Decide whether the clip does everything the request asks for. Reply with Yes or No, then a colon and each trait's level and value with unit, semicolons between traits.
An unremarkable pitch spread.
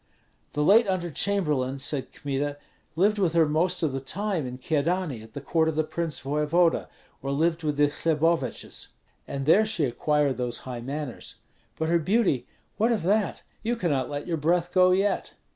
Yes: average, 4.3 semitones